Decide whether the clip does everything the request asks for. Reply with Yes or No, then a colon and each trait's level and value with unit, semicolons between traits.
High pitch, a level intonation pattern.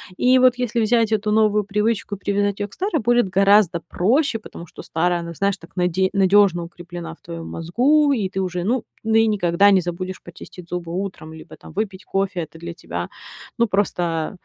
No: high, 195 Hz; average, 3.8 semitones